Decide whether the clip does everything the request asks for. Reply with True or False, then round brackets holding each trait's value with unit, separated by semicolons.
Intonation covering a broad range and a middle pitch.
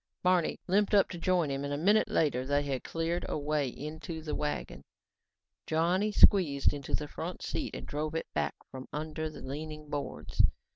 False (3.2 semitones; 155 Hz)